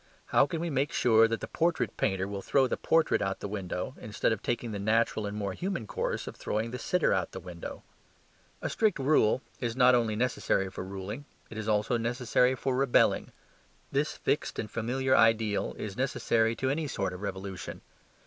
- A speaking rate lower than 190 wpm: No, average, 195 wpm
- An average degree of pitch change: Yes, average, 4.3 semitones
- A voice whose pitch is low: Yes, low, 115 Hz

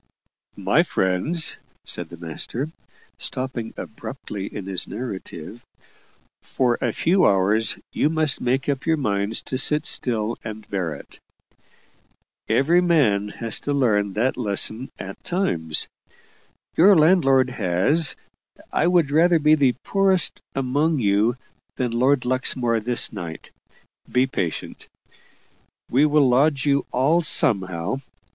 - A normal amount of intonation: No, wide, 6.4 semitones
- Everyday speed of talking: No, slow, 125 wpm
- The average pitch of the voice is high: No, low, 125 Hz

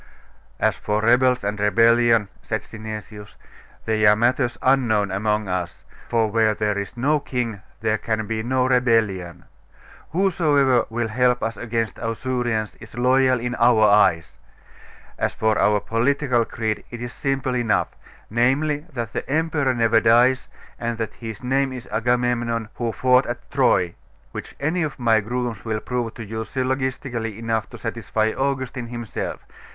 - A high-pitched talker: No, low, 115 Hz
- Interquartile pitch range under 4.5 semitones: Yes, narrow, 2.6 semitones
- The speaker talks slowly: No, average, 155 wpm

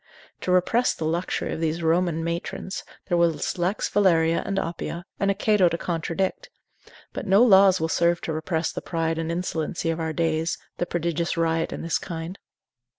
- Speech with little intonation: Yes, narrow, 2.0 semitones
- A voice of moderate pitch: Yes, medium, 170 Hz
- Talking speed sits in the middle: Yes, average, 180 wpm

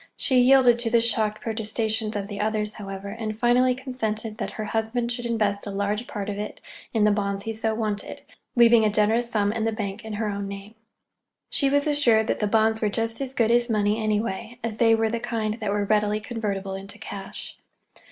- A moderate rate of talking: No, fast, 210 wpm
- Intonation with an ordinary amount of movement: No, narrow, 2.0 semitones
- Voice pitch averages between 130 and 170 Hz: No, high, 220 Hz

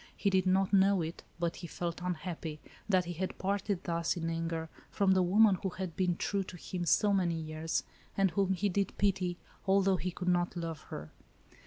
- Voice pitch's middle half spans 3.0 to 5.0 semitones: No, narrow, 2.4 semitones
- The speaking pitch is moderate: Yes, medium, 180 Hz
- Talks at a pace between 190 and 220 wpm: Yes, average, 200 wpm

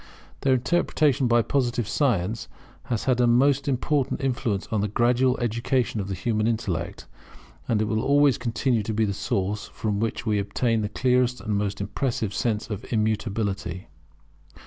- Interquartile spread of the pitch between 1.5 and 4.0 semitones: Yes, average, 3.3 semitones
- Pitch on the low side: Yes, low, 115 Hz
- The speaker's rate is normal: Yes, average, 165 wpm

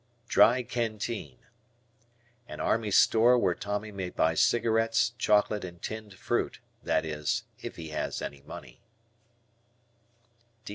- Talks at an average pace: No, slow, 115 wpm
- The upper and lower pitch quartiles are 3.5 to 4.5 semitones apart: Yes, average, 4.1 semitones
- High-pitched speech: No, low, 105 Hz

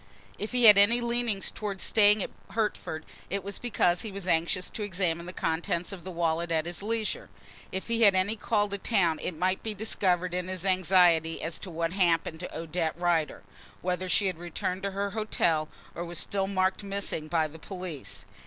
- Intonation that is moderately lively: Yes, average, 3.0 semitones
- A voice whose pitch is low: No, medium, 185 Hz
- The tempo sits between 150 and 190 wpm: No, average, 200 wpm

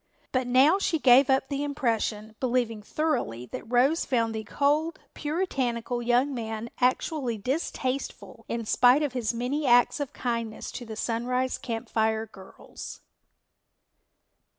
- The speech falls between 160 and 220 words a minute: No, slow, 135 wpm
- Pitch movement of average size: Yes, average, 3.4 semitones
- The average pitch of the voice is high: Yes, high, 245 Hz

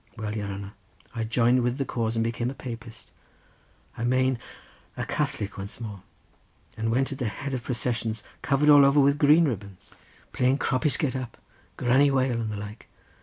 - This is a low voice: Yes, low, 120 Hz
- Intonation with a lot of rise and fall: No, average, 3.3 semitones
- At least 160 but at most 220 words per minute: Yes, average, 180 wpm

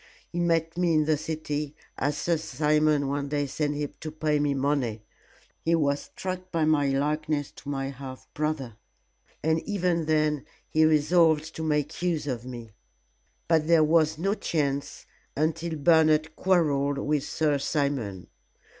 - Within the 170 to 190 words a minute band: No, average, 155 wpm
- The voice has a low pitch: No, medium, 150 Hz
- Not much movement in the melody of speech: Yes, narrow, 2.1 semitones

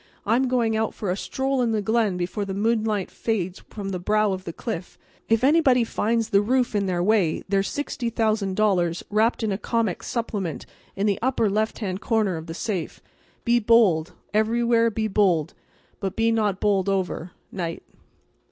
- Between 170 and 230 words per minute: Yes, average, 175 wpm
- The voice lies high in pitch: Yes, high, 215 Hz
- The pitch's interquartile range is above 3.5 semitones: No, average, 3.2 semitones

